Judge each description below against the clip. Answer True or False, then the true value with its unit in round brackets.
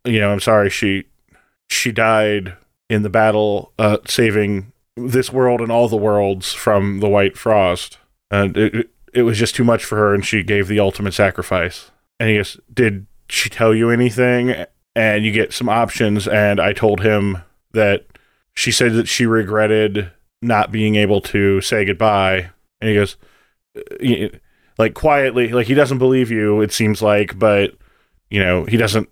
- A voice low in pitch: True (110 Hz)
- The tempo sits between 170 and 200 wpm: True (175 wpm)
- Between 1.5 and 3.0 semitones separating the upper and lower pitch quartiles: True (2.5 semitones)